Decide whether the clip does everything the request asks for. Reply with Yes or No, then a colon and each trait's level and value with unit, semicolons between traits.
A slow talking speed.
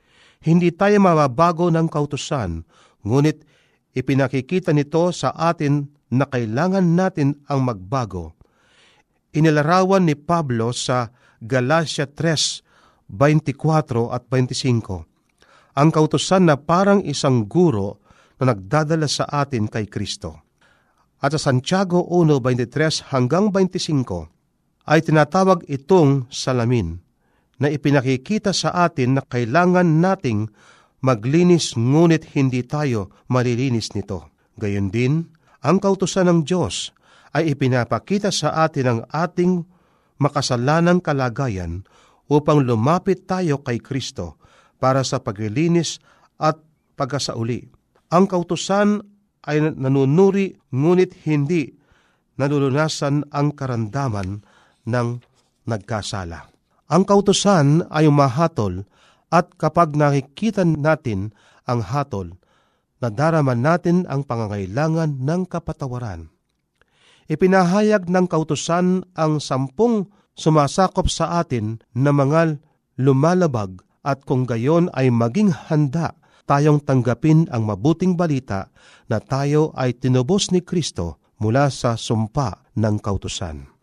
Yes: slow, 105 wpm